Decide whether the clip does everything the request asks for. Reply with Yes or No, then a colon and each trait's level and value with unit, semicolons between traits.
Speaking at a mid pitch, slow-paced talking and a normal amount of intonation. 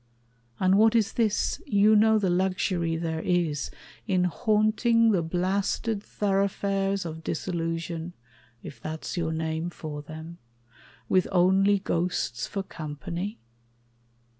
Yes: medium, 180 Hz; slow, 115 wpm; average, 3.5 semitones